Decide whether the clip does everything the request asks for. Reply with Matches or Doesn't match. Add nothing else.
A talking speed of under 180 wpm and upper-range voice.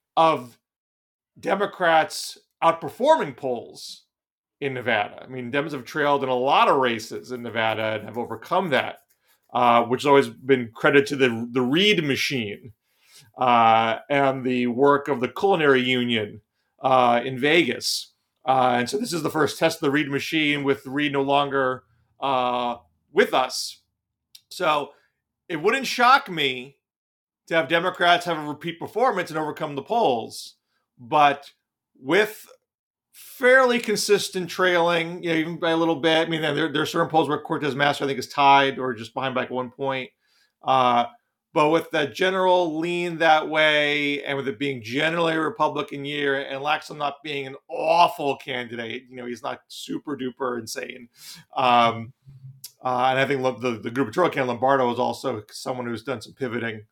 Doesn't match